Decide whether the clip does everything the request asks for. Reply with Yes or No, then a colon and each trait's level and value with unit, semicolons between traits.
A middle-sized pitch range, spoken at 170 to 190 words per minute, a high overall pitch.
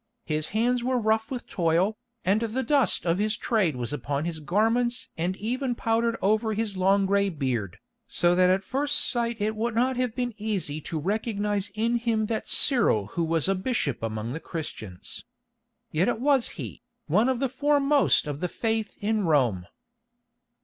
No: wide, 6.0 semitones; average, 175 wpm; high, 210 Hz